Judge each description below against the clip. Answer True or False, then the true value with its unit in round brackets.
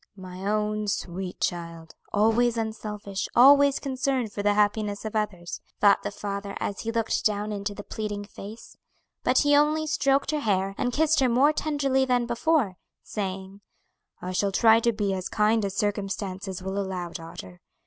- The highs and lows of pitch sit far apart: False (3.6 semitones)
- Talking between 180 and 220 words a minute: False (170 wpm)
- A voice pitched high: True (210 Hz)